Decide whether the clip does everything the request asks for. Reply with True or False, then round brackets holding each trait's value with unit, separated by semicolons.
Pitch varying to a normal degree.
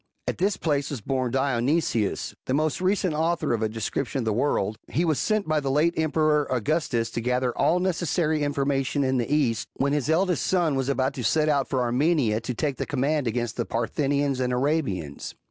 True (4.0 semitones)